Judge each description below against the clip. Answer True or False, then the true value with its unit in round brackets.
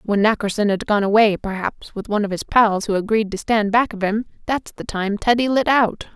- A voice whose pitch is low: False (210 Hz)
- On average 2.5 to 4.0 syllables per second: False (5.4 syllables/s)